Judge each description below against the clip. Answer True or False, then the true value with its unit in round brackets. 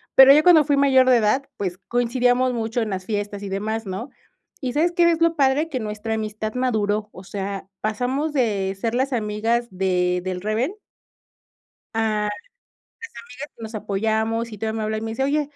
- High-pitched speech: True (225 Hz)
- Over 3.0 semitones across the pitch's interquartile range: True (4.1 semitones)